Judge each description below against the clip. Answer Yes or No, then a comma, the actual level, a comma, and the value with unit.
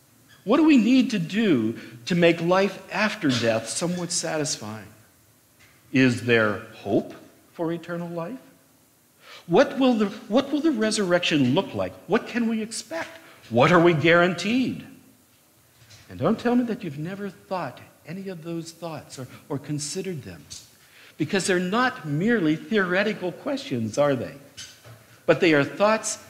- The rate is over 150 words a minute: No, average, 145 wpm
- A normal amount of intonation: No, wide, 8.3 semitones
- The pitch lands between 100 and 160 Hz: No, medium, 175 Hz